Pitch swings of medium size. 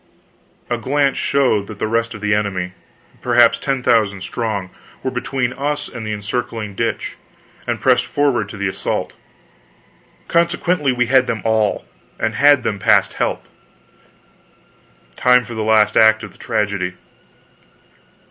Yes: average, 3.7 semitones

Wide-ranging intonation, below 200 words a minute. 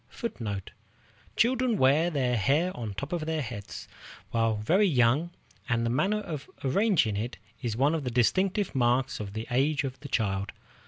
Yes: wide, 6.1 semitones; average, 165 wpm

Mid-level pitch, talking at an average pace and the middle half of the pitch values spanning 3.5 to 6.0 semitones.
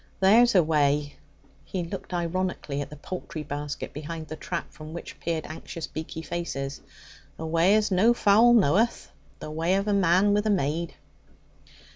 Yes: medium, 170 Hz; average, 165 wpm; average, 4.1 semitones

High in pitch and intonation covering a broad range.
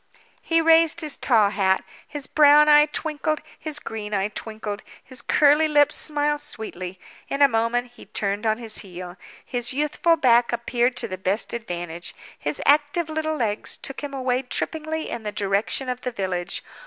Yes: very high, 250 Hz; wide, 6.1 semitones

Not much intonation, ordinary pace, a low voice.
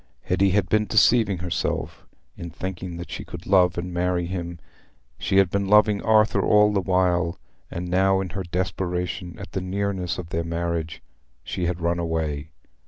Yes: narrow, 2.1 semitones; average, 170 wpm; very low, 90 Hz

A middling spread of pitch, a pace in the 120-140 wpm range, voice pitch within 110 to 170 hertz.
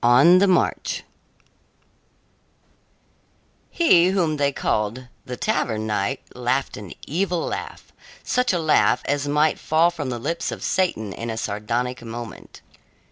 No: wide, 6.5 semitones; slow, 135 wpm; medium, 140 Hz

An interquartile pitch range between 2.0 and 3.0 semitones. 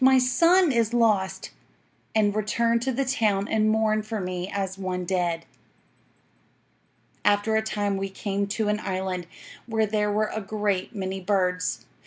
Yes: narrow, 2.5 semitones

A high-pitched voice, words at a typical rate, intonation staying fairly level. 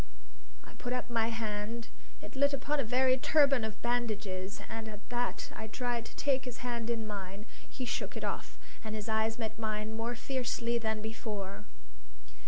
Yes: high, 230 Hz; average, 180 wpm; narrow, 2.2 semitones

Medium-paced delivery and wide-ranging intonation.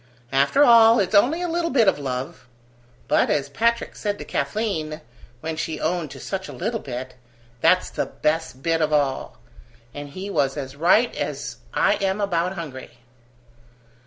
Yes: average, 165 wpm; wide, 6.8 semitones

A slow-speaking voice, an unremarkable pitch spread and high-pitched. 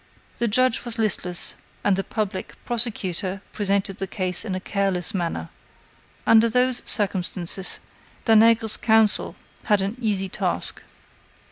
Yes: slow, 125 wpm; average, 3.0 semitones; high, 205 Hz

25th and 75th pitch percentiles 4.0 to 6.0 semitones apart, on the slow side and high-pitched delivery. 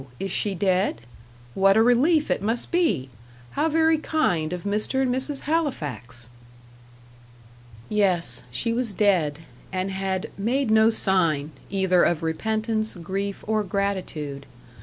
Yes: average, 5.0 semitones; slow, 130 wpm; high, 200 Hz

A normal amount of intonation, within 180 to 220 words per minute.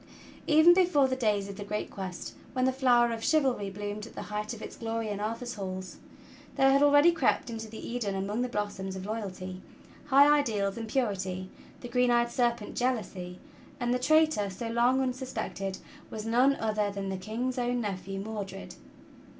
Yes: average, 4.1 semitones; average, 185 wpm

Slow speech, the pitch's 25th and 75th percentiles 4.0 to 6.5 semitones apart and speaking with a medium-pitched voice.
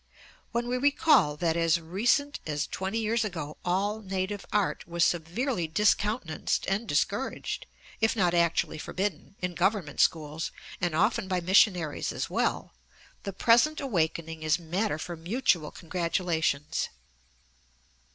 Yes: slow, 130 wpm; average, 4.7 semitones; medium, 180 Hz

